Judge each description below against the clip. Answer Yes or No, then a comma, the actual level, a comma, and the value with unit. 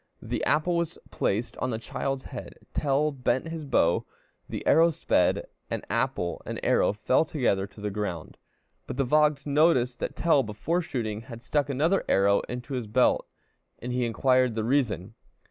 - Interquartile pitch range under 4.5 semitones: No, average, 5.3 semitones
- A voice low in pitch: Yes, low, 125 Hz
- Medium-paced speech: Yes, average, 170 wpm